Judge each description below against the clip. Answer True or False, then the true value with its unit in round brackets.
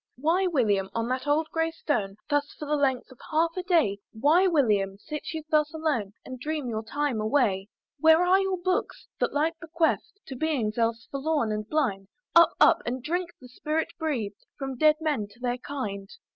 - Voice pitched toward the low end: False (290 Hz)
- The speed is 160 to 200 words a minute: True (190 wpm)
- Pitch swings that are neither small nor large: False (5.8 semitones)